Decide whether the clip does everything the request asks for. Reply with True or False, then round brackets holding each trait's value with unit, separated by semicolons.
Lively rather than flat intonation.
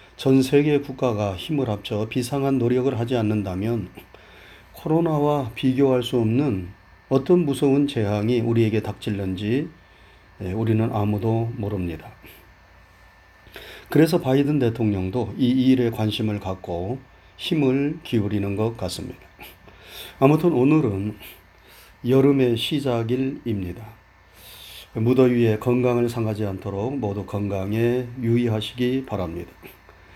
False (4.6 semitones)